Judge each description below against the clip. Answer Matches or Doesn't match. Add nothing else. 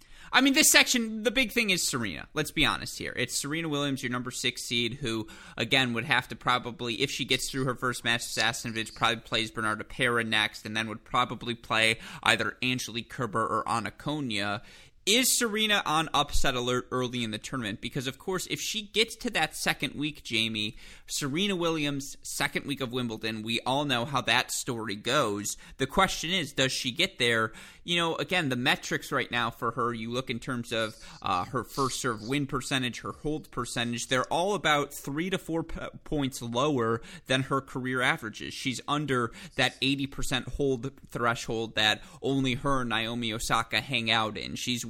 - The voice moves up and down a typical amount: Matches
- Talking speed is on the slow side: Doesn't match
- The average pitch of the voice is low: Matches